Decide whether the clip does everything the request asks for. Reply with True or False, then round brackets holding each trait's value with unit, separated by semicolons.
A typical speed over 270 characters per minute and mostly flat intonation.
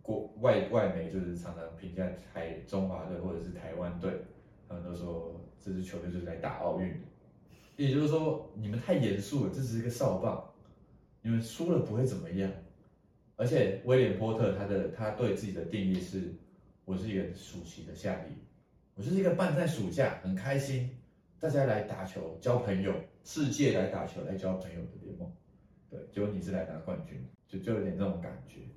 False (280 characters per minute; 5.4 semitones)